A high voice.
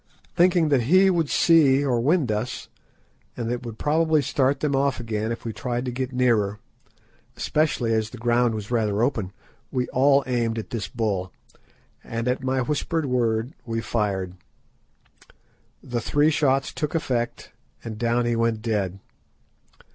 No: low, 120 Hz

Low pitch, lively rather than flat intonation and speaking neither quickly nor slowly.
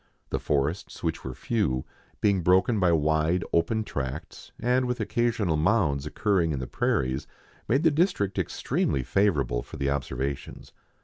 Yes: very low, 85 Hz; wide, 7.5 semitones; average, 145 wpm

